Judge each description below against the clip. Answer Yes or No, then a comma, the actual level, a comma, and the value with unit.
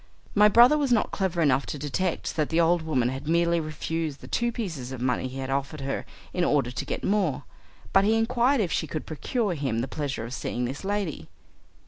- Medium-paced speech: No, fast, 215 wpm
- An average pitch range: No, wide, 6.8 semitones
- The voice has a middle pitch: Yes, medium, 160 Hz